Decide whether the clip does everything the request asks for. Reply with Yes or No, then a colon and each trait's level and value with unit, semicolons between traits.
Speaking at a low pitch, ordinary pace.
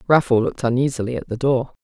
Yes: low, 125 Hz; average, 195 wpm